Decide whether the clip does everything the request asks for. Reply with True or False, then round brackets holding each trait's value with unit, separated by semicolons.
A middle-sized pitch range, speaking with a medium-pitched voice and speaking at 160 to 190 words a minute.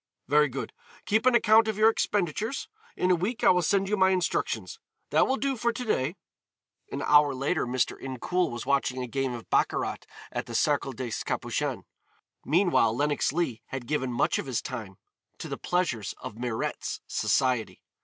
False (7.6 semitones; 150 Hz; 180 wpm)